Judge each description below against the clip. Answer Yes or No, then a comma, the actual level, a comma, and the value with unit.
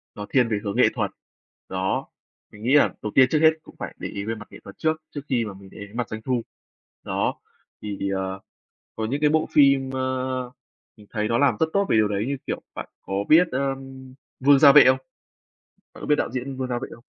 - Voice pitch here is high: No, low, 130 Hz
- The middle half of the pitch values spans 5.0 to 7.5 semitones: No, average, 4.5 semitones